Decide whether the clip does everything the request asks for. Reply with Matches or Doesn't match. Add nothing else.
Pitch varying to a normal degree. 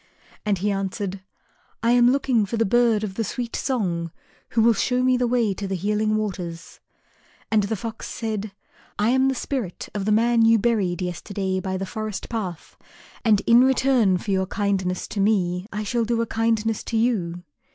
Matches